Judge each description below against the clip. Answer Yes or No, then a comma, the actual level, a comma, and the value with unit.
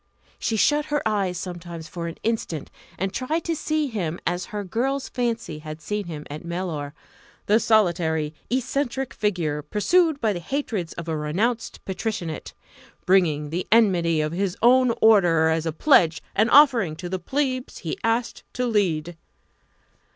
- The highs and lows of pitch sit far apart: Yes, wide, 6.3 semitones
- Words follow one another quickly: No, average, 160 wpm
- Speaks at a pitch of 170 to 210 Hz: Yes, high, 190 Hz